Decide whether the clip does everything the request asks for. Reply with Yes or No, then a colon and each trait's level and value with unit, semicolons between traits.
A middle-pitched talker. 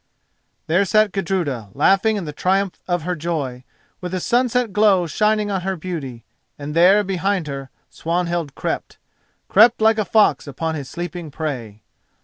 Yes: medium, 180 Hz